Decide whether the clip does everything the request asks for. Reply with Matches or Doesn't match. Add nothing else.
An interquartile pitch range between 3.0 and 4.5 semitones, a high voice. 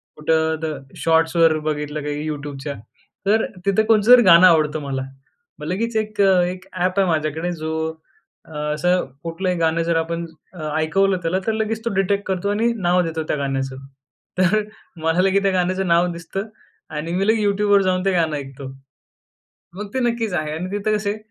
Doesn't match